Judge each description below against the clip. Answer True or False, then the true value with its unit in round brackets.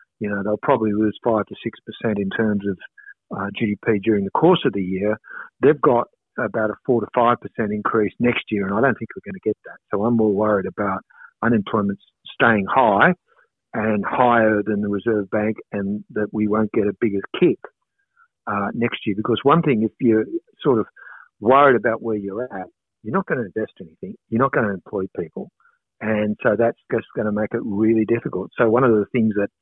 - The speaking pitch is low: True (110 Hz)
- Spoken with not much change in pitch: True (2.1 semitones)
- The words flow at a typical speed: False (215 wpm)